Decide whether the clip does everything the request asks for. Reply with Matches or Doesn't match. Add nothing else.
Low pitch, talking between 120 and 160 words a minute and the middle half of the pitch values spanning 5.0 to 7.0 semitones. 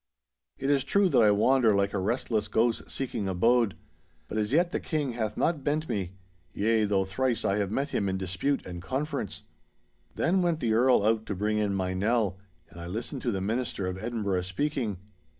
Doesn't match